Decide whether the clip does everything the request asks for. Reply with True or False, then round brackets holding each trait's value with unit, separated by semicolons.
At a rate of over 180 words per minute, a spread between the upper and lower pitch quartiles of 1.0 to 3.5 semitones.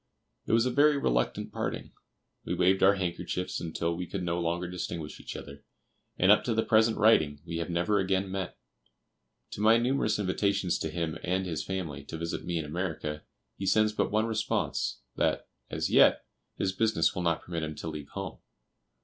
False (190 wpm; 4.1 semitones)